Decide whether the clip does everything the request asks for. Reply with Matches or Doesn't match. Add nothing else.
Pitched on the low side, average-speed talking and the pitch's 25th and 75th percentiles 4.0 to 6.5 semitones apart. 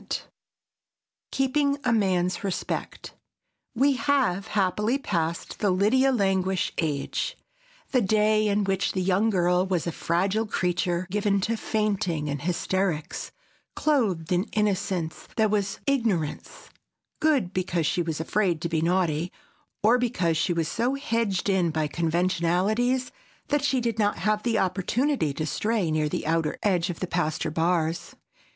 Doesn't match